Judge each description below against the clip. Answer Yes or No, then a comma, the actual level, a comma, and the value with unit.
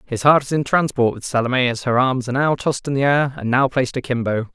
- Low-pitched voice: Yes, low, 130 Hz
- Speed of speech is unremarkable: No, fast, 265 wpm